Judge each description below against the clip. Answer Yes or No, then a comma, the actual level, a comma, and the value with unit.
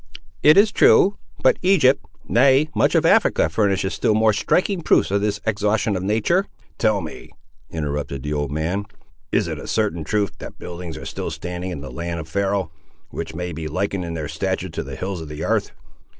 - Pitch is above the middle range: No, very low, 95 Hz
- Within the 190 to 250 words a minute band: Yes, average, 195 wpm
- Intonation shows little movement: No, average, 5.1 semitones